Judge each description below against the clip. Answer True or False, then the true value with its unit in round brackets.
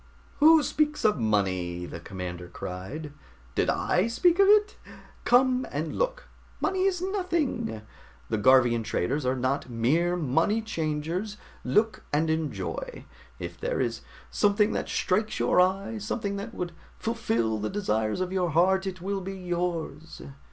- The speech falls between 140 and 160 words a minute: True (145 wpm)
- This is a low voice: False (180 Hz)